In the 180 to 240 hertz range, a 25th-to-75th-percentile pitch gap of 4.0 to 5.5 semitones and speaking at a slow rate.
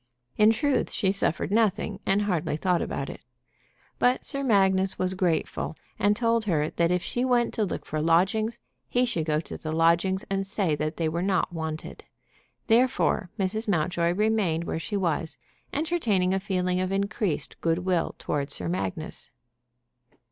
No: high, 190 Hz; average, 4.4 semitones; average, 165 wpm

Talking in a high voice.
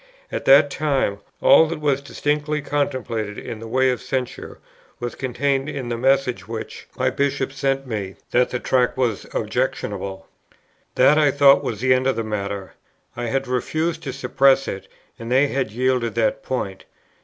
No: low, 130 Hz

